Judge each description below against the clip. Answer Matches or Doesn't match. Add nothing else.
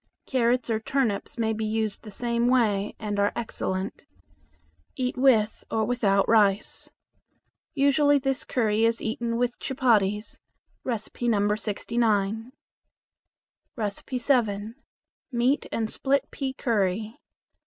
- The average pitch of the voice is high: Matches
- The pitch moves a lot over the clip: Doesn't match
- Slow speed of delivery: Matches